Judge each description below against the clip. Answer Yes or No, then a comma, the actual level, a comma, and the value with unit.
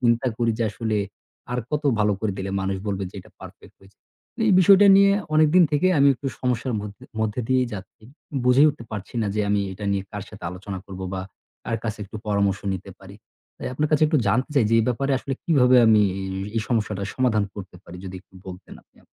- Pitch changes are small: No, average, 4.6 semitones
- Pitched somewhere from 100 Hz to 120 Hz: Yes, low, 110 Hz